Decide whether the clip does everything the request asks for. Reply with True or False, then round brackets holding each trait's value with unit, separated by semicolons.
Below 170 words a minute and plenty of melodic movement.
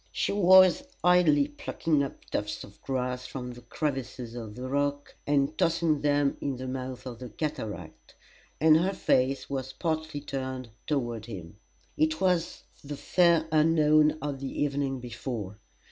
False (150 wpm; 3.7 semitones)